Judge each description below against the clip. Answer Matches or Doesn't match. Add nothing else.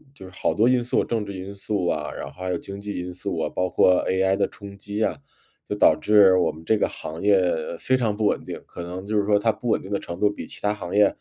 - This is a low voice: Matches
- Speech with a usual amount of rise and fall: Doesn't match